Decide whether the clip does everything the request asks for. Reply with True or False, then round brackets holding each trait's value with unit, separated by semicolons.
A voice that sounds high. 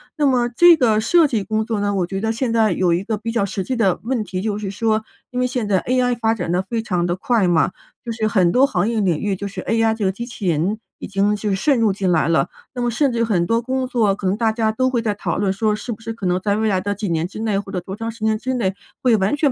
True (215 Hz)